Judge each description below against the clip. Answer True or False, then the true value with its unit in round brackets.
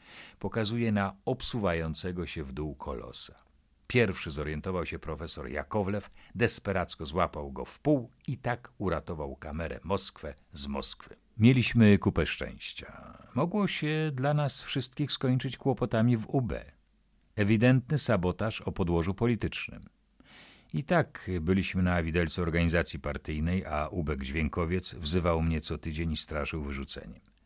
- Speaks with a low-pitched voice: True (90 Hz)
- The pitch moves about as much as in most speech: False (6.3 semitones)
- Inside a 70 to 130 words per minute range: True (125 wpm)